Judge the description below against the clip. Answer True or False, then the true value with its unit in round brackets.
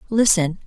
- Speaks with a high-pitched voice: True (195 Hz)